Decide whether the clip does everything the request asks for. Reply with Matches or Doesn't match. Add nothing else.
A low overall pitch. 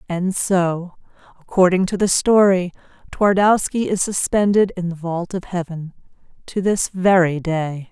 Doesn't match